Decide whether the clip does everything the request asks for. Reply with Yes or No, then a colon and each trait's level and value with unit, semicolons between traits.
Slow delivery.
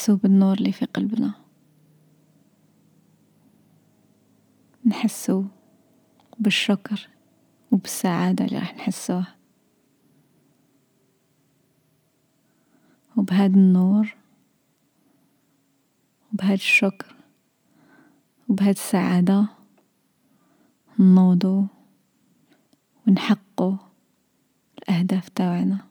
Yes: slow, 50 wpm